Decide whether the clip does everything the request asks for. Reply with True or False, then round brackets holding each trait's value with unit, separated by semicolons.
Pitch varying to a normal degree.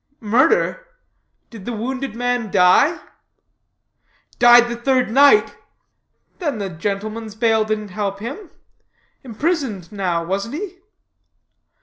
True (4.5 semitones)